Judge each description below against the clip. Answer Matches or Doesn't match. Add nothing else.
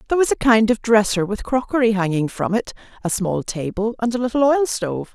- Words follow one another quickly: Matches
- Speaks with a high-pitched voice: Matches